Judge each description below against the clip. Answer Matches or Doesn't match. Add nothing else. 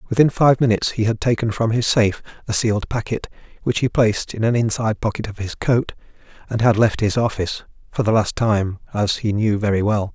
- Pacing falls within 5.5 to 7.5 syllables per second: Matches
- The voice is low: Matches